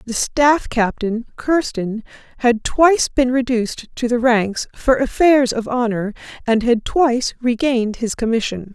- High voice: Yes, high, 240 Hz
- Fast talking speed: No, average, 145 wpm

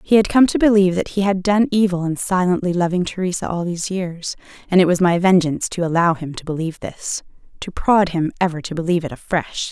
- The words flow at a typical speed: No, fast, 220 wpm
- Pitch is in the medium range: Yes, medium, 180 Hz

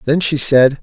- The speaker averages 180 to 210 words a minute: No, fast, 220 wpm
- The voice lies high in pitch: No, medium, 145 Hz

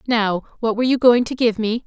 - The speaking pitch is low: No, high, 230 Hz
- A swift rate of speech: Yes, fast, 260 wpm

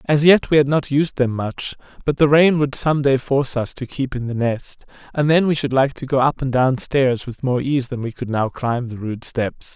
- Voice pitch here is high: No, low, 135 Hz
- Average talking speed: No, fast, 265 wpm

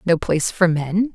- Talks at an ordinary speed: No, fast, 210 wpm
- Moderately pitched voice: Yes, medium, 180 Hz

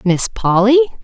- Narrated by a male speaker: No, female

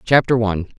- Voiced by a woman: No, male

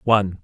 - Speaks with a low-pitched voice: Yes, low, 100 Hz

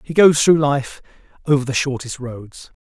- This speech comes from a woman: No, male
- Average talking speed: Yes, average, 170 wpm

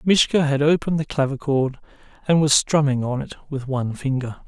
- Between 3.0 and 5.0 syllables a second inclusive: No, 5.7 syllables/s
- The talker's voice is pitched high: No, medium, 140 Hz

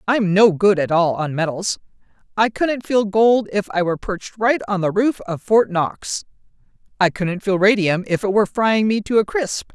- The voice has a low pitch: No, high, 200 Hz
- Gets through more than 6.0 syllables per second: No, 4.8 syllables/s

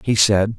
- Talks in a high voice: No, low, 105 Hz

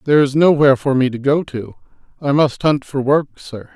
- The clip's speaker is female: No, male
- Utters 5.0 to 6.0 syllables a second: Yes, 5.4 syllables/s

